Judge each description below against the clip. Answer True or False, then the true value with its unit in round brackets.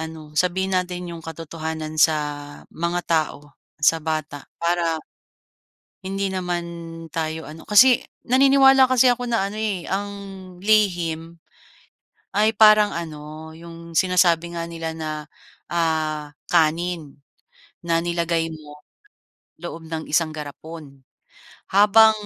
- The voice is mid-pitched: True (170 Hz)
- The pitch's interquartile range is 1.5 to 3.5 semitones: True (3.0 semitones)